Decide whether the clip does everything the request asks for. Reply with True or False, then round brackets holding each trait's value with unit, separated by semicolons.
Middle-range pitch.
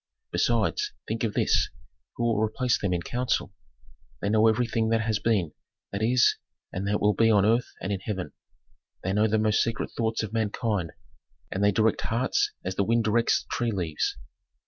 False (110 Hz)